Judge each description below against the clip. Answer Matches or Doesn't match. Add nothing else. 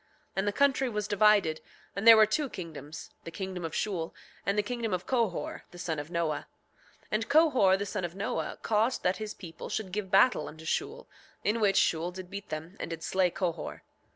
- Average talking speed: Doesn't match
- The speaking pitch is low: Doesn't match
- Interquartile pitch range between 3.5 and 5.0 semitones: Matches